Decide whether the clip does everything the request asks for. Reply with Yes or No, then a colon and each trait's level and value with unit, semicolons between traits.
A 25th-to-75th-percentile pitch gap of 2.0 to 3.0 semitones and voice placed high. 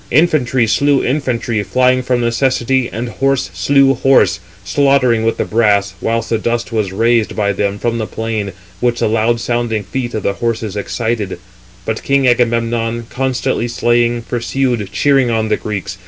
No: narrow, 2.6 semitones; low, 115 Hz